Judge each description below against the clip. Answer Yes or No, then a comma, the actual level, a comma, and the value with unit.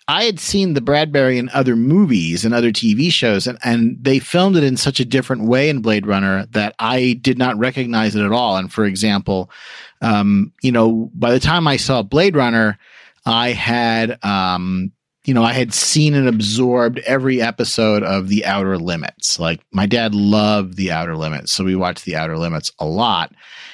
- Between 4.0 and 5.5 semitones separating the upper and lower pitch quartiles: Yes, average, 4.6 semitones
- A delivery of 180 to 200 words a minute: Yes, average, 195 wpm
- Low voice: Yes, low, 115 Hz